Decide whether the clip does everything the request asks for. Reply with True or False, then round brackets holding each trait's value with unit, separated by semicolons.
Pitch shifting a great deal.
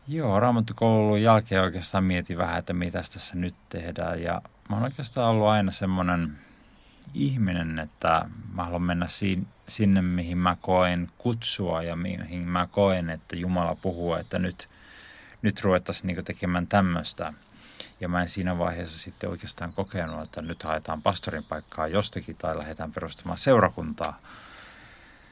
False (2.7 semitones)